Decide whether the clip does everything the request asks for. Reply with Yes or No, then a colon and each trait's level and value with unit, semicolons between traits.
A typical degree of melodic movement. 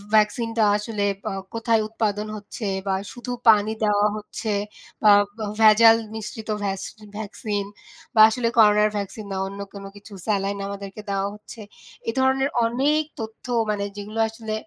No: narrow, 1.7 semitones